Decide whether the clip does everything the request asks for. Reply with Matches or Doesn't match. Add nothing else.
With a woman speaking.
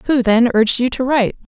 Matches